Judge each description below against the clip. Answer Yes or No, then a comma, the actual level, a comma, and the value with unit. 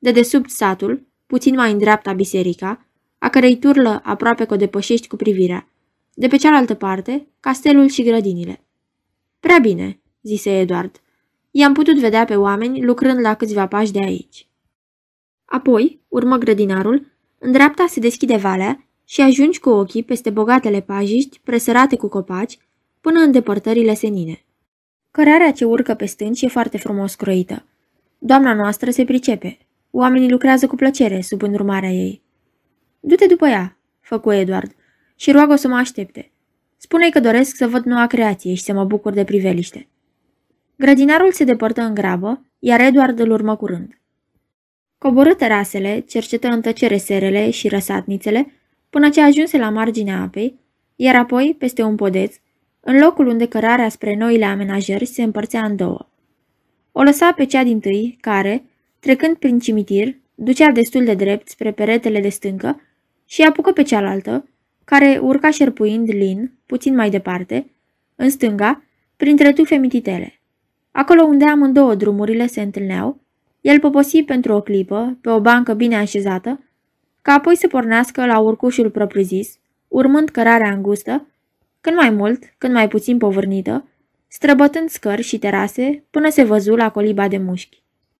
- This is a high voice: Yes, high, 235 Hz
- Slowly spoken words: No, average, 150 wpm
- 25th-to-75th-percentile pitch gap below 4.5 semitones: No, average, 4.8 semitones